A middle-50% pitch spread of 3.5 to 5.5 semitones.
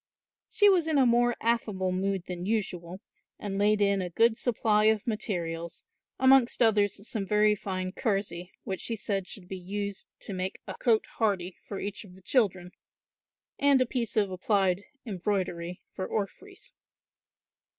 No: average, 3.1 semitones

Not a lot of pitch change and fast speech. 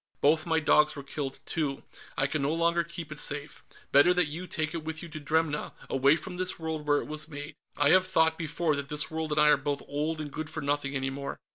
Yes: narrow, 2.0 semitones; fast, 250 wpm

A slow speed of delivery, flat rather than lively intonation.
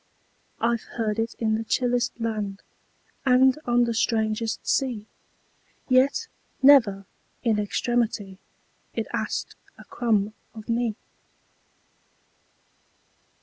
Yes: slow, 105 wpm; narrow, 2.2 semitones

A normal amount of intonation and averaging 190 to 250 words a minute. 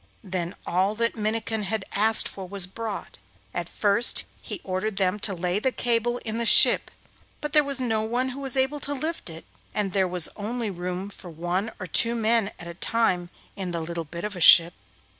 Yes: average, 4.3 semitones; fast, 205 wpm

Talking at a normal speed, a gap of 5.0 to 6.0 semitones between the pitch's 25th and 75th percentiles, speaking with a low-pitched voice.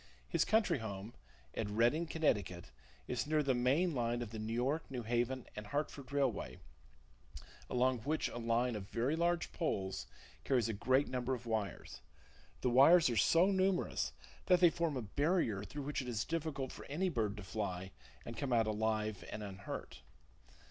Yes: average, 175 wpm; wide, 5.4 semitones; low, 125 Hz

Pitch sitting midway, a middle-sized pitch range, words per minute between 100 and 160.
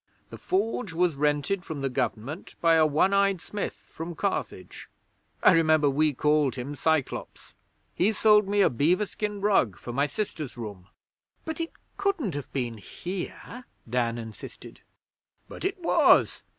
No: medium, 160 Hz; wide, 6.5 semitones; average, 150 wpm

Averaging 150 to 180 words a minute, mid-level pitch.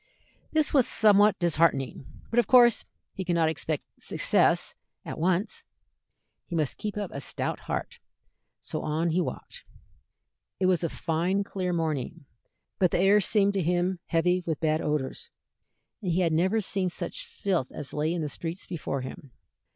Yes: average, 165 wpm; medium, 175 Hz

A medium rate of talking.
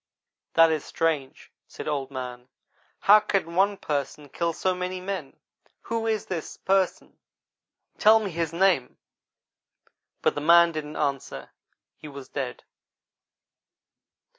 No: slow, 125 wpm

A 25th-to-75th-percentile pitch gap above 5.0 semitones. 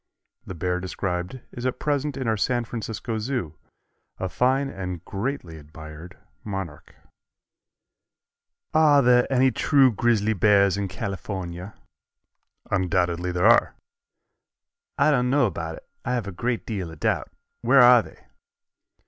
Yes: wide, 5.6 semitones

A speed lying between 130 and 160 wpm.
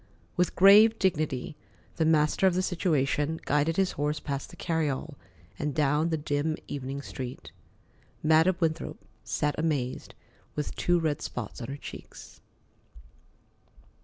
Yes: slow, 135 wpm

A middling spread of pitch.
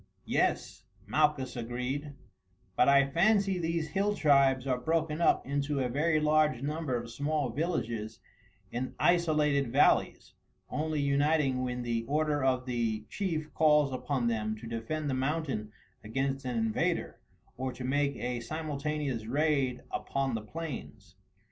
Yes: average, 3.6 semitones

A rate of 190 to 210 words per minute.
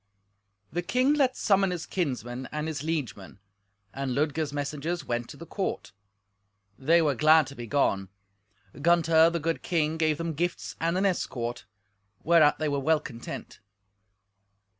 No: average, 150 wpm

